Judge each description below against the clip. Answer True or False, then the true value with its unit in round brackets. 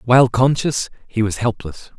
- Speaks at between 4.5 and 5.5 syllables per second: True (4.9 syllables/s)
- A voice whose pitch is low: True (115 Hz)